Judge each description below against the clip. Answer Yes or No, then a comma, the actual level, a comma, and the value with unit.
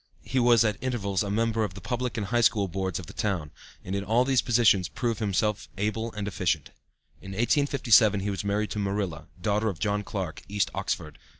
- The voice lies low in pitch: Yes, low, 105 Hz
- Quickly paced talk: Yes, fast, 210 wpm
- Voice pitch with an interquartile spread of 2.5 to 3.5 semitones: Yes, average, 2.9 semitones